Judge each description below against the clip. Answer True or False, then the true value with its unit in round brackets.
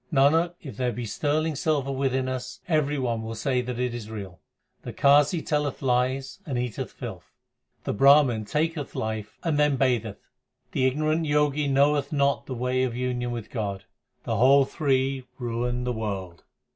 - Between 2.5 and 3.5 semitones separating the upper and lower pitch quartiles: True (3.1 semitones)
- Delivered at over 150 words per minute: True (165 wpm)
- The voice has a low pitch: True (130 Hz)